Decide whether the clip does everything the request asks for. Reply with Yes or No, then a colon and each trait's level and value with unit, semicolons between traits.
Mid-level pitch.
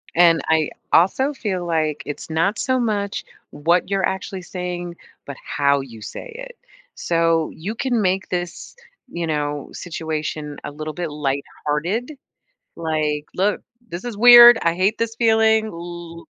Yes: medium, 175 Hz